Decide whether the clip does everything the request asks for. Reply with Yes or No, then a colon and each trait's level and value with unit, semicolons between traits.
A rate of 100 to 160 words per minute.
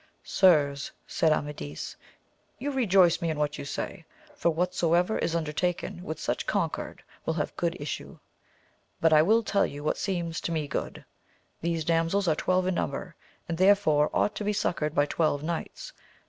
No: average, 175 wpm